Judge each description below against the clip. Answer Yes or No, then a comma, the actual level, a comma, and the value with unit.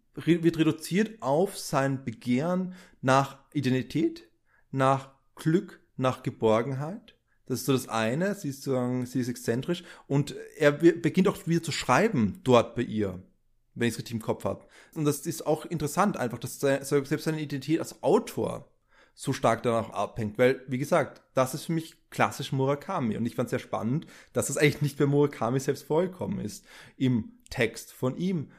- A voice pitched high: No, medium, 140 Hz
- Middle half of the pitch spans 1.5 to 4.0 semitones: No, average, 4.4 semitones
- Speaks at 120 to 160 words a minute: No, average, 175 wpm